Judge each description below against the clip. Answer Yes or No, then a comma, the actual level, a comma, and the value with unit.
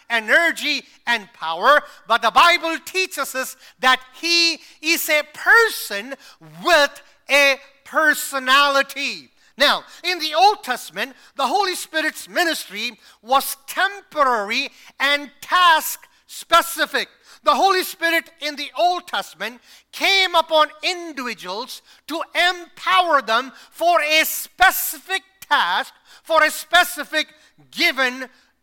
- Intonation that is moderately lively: Yes, average, 4.3 semitones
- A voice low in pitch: No, very high, 300 Hz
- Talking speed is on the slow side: Yes, slow, 105 wpm